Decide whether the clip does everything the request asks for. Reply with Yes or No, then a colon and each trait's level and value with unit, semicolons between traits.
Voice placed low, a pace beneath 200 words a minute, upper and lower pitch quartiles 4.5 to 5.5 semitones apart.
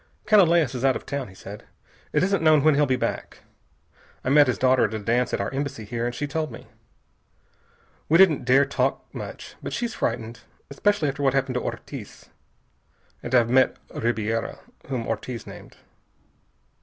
No: low, 130 Hz; average, 180 wpm; average, 3.7 semitones